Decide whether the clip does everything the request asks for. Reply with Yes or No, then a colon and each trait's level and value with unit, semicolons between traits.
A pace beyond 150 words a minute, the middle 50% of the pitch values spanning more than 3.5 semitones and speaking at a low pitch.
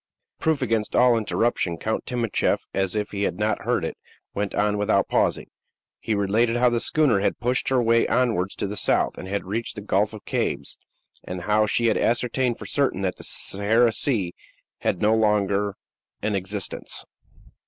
No: average, 180 wpm; average, 3.0 semitones; low, 105 Hz